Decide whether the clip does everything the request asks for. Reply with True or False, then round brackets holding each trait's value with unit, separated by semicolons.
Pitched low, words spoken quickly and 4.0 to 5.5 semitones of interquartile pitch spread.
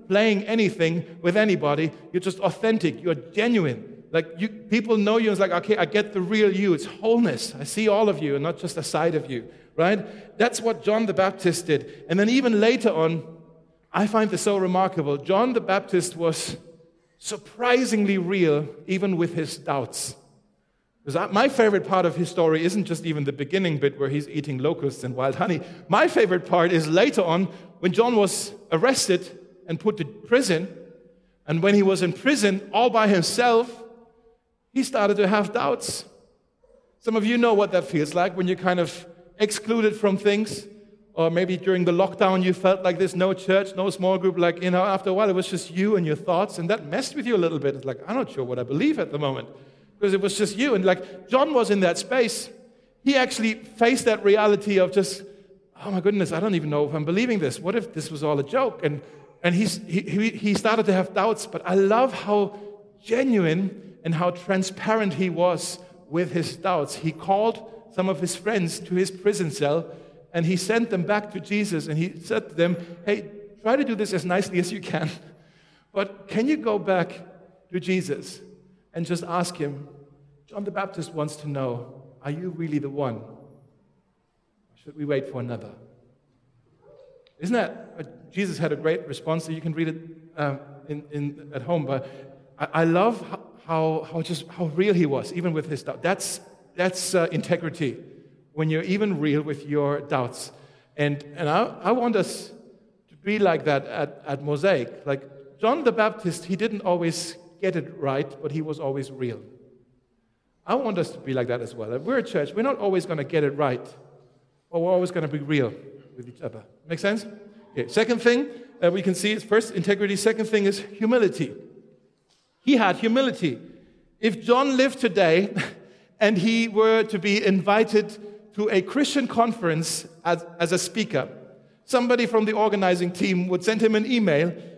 False (185 Hz; 195 wpm; 4.6 semitones)